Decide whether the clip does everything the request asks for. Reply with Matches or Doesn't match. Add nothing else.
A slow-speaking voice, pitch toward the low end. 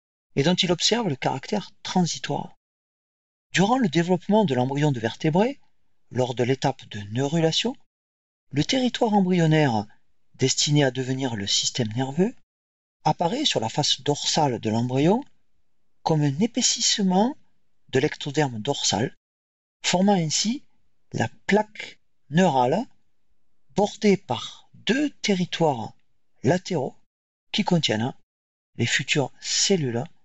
Doesn't match